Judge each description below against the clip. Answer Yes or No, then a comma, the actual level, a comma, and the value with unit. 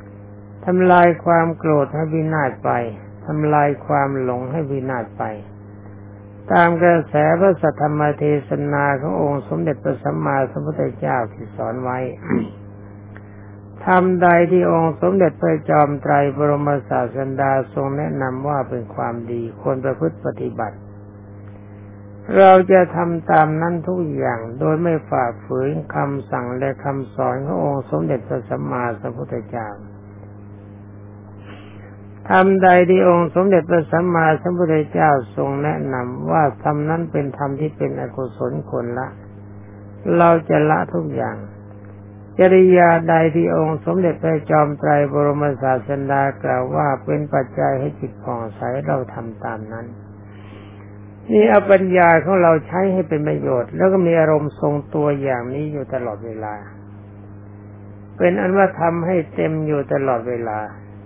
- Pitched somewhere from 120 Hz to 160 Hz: Yes, low, 135 Hz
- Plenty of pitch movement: Yes, wide, 7.7 semitones